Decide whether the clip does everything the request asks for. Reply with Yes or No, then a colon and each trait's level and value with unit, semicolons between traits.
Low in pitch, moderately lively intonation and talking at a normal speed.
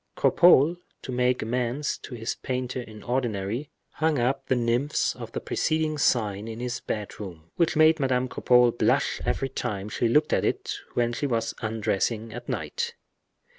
Yes: low, 125 Hz; average, 3.3 semitones; average, 165 wpm